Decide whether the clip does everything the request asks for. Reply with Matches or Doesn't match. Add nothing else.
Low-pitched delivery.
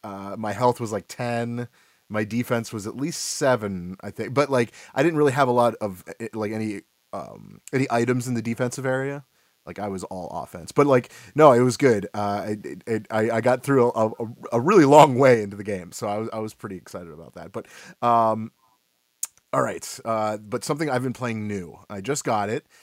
Matches